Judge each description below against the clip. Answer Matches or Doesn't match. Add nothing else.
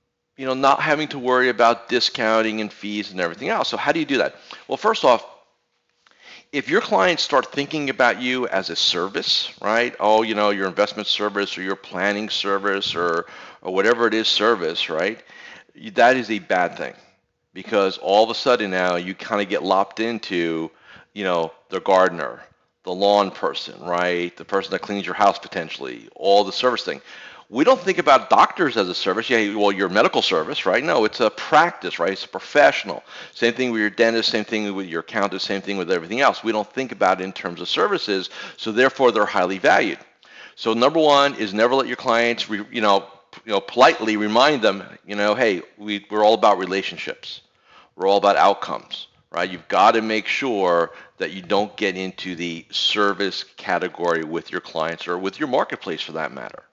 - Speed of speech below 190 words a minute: Doesn't match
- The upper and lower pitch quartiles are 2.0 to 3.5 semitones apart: Matches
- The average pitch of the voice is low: Matches